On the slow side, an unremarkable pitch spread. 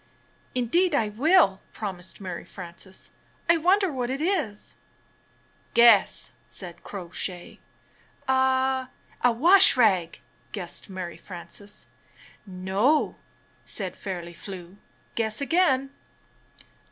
No: slow, 105 wpm; wide, 6.3 semitones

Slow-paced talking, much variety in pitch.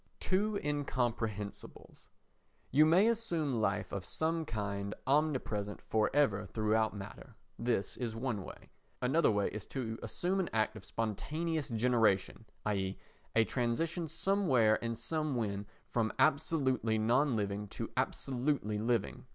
Yes: slow, 125 wpm; wide, 5.9 semitones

